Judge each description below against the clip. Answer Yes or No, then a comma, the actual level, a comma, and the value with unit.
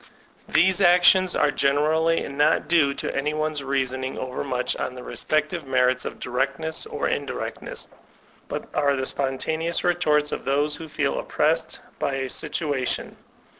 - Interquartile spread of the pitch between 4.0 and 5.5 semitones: No, average, 3.0 semitones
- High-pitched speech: No, medium, 145 Hz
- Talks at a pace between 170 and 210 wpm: No, average, 145 wpm